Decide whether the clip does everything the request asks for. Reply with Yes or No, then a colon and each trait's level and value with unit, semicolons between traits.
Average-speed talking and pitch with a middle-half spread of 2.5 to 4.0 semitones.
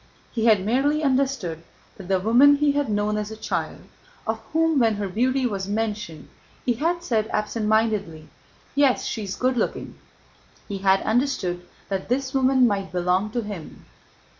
No: average, 165 wpm; average, 4.8 semitones